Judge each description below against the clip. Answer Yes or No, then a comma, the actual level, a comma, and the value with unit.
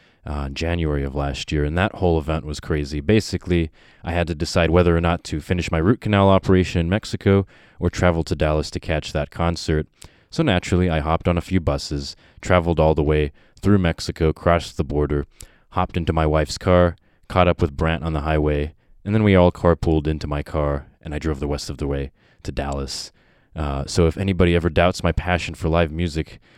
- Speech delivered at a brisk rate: Yes, fast, 210 wpm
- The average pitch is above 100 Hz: No, very low, 85 Hz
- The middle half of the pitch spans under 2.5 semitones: No, average, 2.9 semitones